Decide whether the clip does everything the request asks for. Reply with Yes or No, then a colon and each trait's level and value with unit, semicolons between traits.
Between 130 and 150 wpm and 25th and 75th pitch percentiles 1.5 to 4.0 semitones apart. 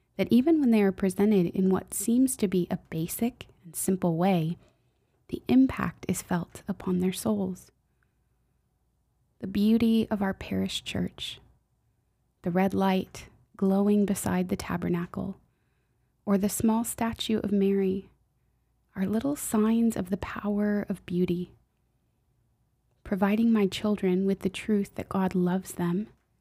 Yes: slow, 135 wpm; average, 2.8 semitones